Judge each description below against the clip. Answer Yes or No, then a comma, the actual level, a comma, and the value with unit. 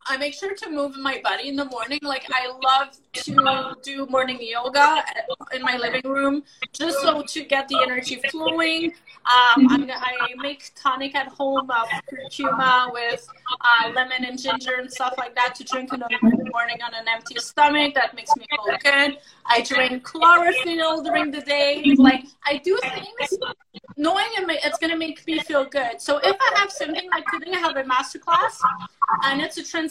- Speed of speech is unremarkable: Yes, average, 185 wpm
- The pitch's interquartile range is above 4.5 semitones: No, average, 3.7 semitones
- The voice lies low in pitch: No, very high, 275 Hz